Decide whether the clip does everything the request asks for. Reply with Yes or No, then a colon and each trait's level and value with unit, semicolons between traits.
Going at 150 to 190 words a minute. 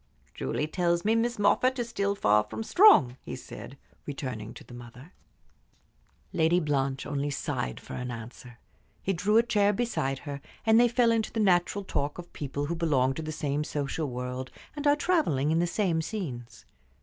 Yes: average, 180 wpm